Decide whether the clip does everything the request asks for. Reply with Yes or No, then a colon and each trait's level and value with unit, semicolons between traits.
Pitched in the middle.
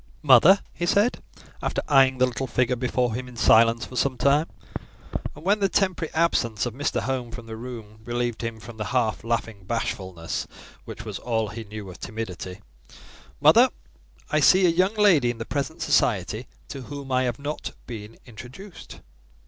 No: low, 125 Hz